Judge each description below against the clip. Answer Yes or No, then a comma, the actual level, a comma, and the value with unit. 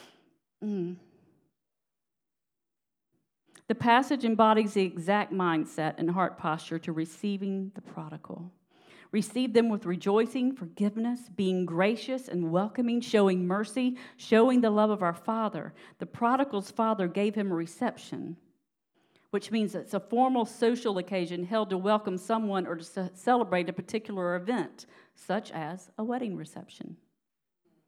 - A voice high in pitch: Yes, high, 200 Hz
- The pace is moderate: No, slow, 130 wpm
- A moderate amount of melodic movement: Yes, average, 3.9 semitones